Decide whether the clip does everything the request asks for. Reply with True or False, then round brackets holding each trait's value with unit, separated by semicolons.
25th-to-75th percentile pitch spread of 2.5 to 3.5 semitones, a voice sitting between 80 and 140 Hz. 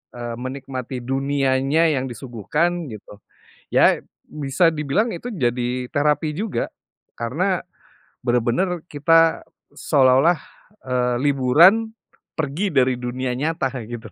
False (4.5 semitones; 135 Hz)